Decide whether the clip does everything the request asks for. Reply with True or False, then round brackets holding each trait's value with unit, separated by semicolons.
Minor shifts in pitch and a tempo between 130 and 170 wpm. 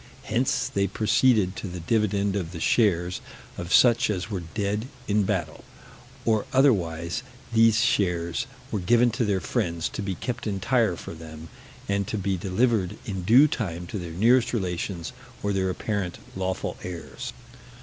False (4.1 semitones; 160 wpm)